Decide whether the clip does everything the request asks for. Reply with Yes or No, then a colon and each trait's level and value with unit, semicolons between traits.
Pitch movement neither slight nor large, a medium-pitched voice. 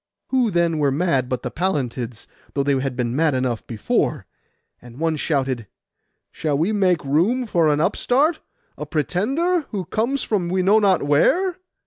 No: wide, 7.6 semitones; medium, 165 Hz